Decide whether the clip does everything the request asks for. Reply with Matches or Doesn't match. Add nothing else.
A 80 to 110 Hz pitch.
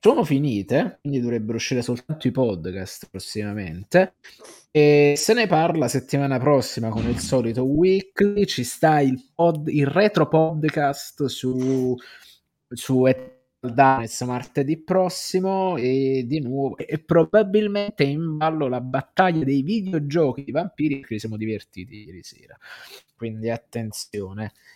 Doesn't match